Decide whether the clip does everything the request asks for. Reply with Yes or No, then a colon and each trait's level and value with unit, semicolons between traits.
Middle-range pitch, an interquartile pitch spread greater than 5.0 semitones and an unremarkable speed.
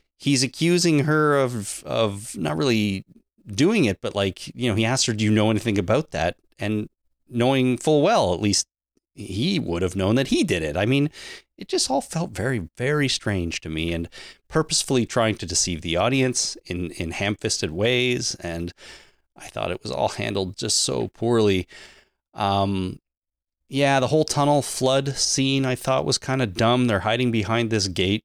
No: low, 115 Hz; wide, 5.5 semitones; average, 185 wpm